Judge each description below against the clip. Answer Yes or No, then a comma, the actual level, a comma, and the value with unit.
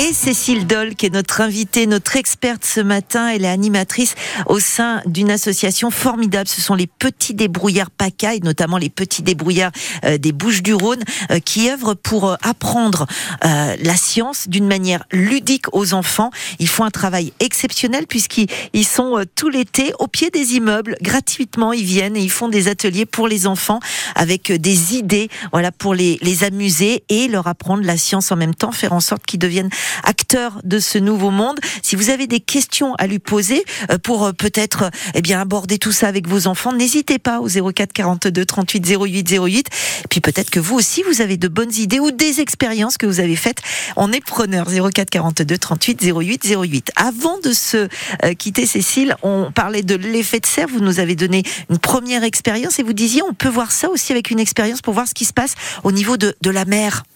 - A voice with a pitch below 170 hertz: No, high, 210 Hz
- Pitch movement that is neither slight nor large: Yes, average, 3.9 semitones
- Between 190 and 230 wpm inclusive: Yes, average, 205 wpm